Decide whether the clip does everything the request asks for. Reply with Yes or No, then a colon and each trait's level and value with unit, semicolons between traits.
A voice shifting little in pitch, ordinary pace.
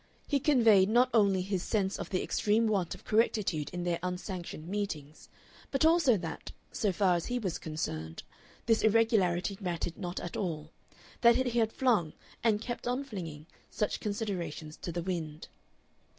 No: average, 4.7 semitones; average, 165 wpm